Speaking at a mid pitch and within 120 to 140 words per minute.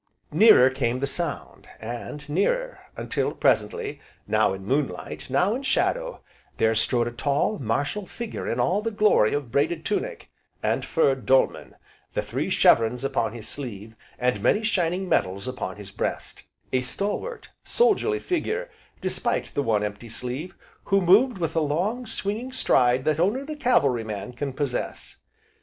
No: medium, 145 Hz; average, 155 wpm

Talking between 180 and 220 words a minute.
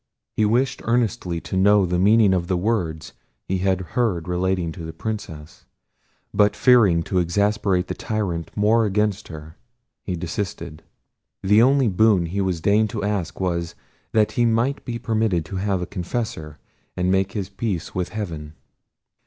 No: average, 160 wpm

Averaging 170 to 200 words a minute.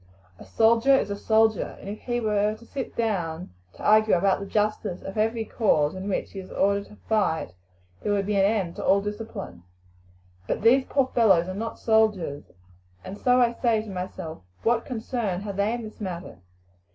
Yes: average, 195 wpm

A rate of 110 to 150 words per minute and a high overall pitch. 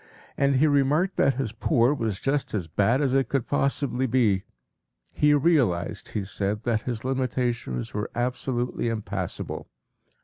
No: average, 145 wpm; low, 125 Hz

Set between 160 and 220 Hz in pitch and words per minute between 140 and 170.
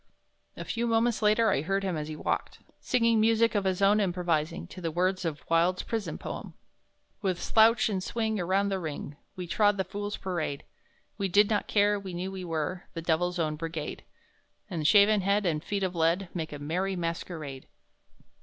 No: medium, 185 Hz; average, 190 wpm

